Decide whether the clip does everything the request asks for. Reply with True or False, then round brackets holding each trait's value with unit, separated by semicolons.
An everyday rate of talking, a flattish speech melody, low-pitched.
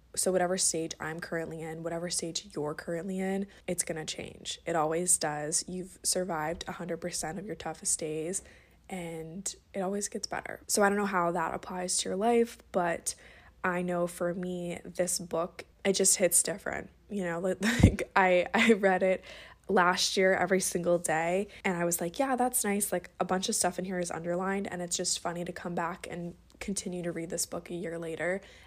False (195 wpm; 2.1 semitones; 180 Hz)